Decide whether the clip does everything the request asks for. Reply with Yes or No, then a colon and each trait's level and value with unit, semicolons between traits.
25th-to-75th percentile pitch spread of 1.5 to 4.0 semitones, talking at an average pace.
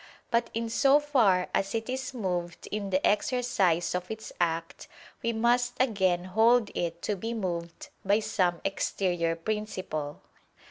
No: average, 4.7 semitones; average, 145 wpm